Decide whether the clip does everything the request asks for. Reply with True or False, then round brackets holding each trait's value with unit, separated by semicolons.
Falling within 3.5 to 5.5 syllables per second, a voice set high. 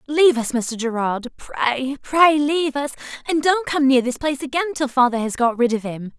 True (5.2 syllables/s; 270 Hz)